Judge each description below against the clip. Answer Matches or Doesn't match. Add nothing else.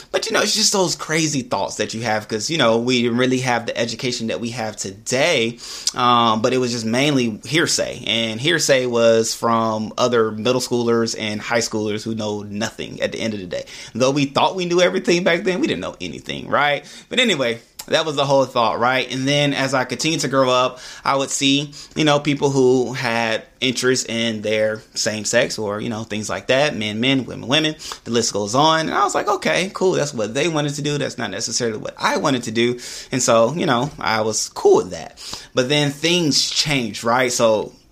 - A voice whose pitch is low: Matches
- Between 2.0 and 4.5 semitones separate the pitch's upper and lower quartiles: Matches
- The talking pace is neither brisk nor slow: Doesn't match